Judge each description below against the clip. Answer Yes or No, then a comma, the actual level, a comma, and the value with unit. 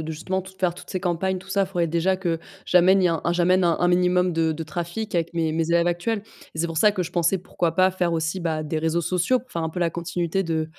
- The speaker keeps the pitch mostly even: Yes, narrow, 2.0 semitones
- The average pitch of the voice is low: No, medium, 175 Hz